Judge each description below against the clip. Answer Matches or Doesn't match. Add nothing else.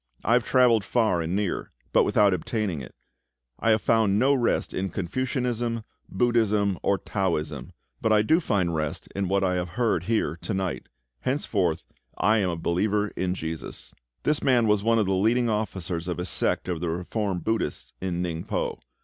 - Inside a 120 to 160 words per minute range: Doesn't match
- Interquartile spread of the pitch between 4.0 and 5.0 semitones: Matches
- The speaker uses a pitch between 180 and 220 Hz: Doesn't match